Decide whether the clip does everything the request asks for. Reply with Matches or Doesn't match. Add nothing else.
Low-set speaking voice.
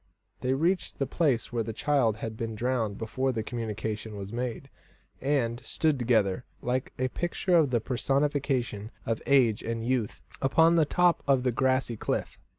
Matches